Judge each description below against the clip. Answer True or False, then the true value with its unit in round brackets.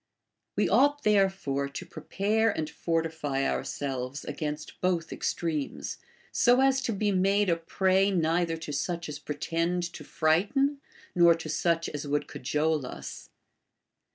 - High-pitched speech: False (165 Hz)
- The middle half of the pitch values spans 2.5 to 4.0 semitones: False (4.5 semitones)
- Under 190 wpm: True (135 wpm)